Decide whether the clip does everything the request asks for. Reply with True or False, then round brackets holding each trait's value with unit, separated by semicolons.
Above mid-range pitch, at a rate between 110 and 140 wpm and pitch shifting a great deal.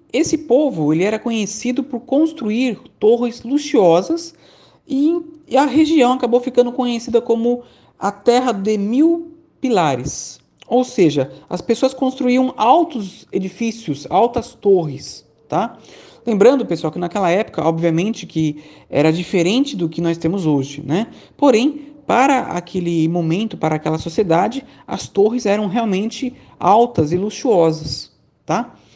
True (230 Hz; 125 wpm; 7.0 semitones)